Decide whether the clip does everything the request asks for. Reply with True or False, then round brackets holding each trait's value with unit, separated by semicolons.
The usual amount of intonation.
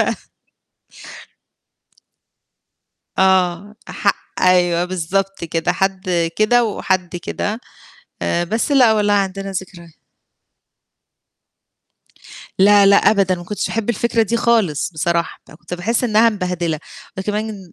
True (3.2 semitones)